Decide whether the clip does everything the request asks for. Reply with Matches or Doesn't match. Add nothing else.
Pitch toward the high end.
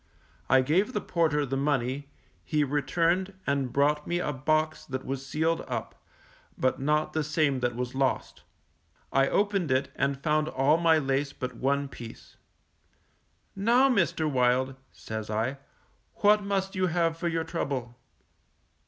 Doesn't match